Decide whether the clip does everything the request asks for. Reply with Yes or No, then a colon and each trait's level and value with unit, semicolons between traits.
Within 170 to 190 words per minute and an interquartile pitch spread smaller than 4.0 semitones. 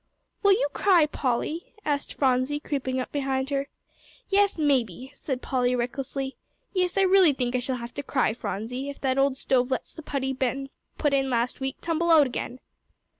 Yes: average, 180 wpm; narrow, 2.6 semitones